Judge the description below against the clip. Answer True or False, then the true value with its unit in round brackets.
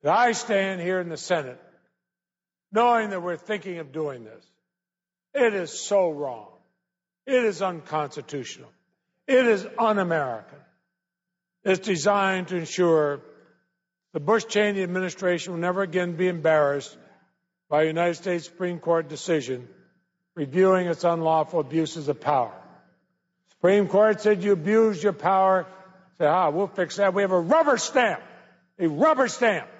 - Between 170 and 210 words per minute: False (135 wpm)